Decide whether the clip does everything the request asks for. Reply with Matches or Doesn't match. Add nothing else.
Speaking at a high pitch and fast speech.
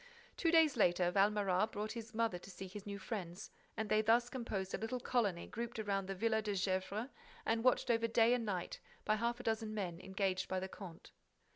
Matches